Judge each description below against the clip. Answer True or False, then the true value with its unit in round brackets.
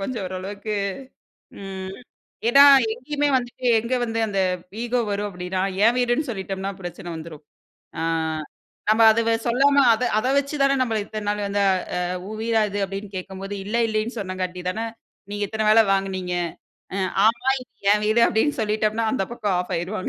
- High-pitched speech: True (215 Hz)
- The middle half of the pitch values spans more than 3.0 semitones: True (3.4 semitones)